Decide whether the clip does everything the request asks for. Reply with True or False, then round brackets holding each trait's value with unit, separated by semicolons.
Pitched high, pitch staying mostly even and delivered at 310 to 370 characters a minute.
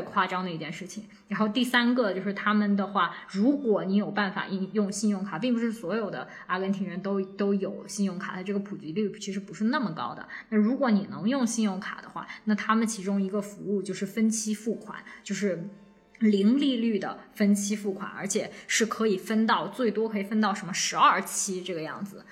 True (205 Hz; 1.9 semitones; 315 characters per minute)